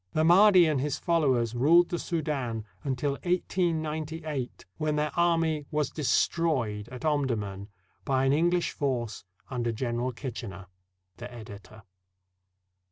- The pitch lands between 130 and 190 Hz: Yes, medium, 140 Hz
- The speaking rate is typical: No, slow, 125 wpm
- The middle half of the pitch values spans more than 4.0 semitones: Yes, average, 5.0 semitones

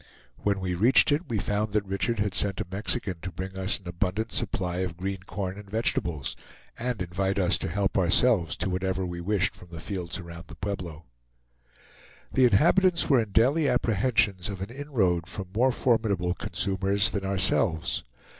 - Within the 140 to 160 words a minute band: No, average, 175 wpm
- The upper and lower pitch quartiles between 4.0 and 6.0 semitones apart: No, average, 3.5 semitones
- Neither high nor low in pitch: No, very low, 95 Hz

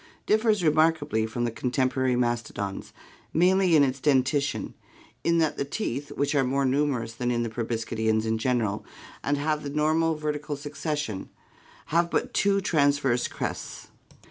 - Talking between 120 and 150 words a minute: Yes, average, 145 wpm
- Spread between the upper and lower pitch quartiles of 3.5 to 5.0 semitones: Yes, average, 4.3 semitones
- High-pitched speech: No, medium, 140 Hz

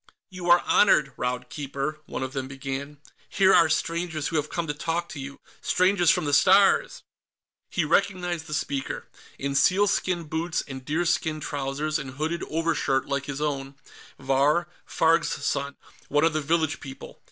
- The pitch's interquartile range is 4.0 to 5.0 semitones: No, average, 3.6 semitones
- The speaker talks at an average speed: Yes, average, 165 wpm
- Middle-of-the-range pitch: Yes, medium, 155 Hz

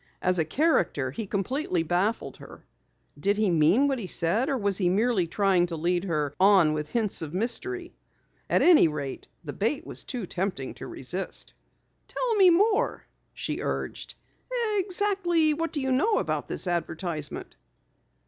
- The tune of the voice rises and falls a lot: Yes, wide, 8.9 semitones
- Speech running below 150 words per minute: No, average, 160 wpm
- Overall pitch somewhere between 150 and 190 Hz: No, high, 200 Hz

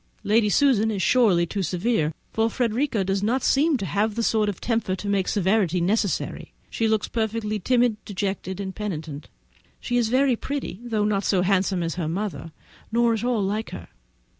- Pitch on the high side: Yes, high, 210 Hz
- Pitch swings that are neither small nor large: Yes, average, 3.2 semitones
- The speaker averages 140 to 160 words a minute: No, average, 185 wpm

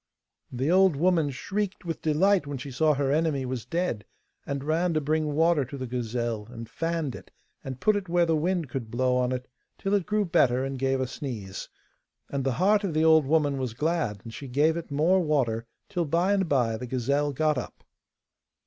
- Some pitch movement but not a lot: Yes, average, 4.8 semitones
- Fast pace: Yes, fast, 210 wpm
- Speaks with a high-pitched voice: No, medium, 145 Hz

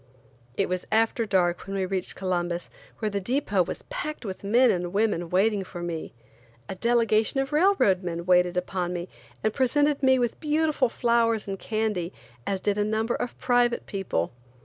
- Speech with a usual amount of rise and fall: Yes, average, 4.8 semitones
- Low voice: No, high, 210 Hz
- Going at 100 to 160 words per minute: No, average, 175 wpm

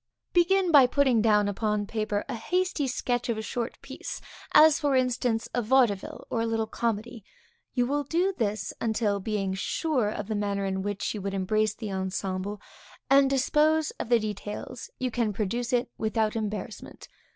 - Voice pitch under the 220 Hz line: No, high, 225 Hz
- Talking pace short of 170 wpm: No, average, 175 wpm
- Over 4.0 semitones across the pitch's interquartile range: No, average, 3.7 semitones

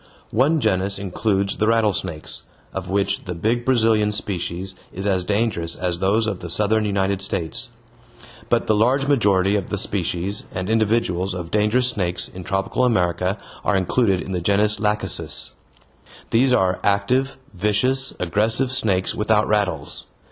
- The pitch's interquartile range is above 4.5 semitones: No, average, 3.0 semitones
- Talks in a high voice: No, low, 100 Hz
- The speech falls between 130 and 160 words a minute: Yes, average, 150 wpm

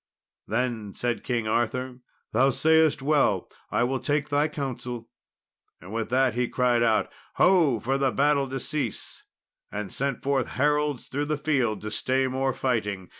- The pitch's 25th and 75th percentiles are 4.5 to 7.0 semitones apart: No, average, 3.3 semitones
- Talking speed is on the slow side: No, average, 160 wpm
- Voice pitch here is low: Yes, low, 130 Hz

